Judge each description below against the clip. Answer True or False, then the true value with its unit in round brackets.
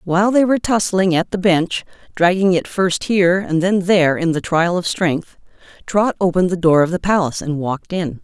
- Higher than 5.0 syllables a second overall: True (5.5 syllables/s)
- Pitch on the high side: False (180 Hz)